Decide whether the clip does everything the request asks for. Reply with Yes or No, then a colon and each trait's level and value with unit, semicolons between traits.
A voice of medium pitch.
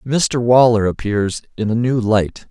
No: low, 115 Hz